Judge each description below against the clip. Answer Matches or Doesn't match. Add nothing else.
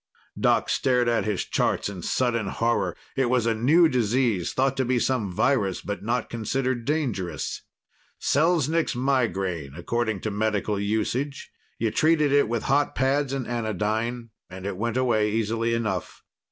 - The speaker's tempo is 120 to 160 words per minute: Matches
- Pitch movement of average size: Matches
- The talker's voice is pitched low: Matches